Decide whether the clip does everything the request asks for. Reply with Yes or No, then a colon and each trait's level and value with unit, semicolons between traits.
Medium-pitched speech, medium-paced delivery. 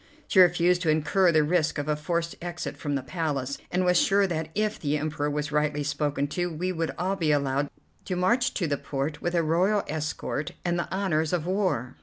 No: medium, 160 Hz; fast, 215 wpm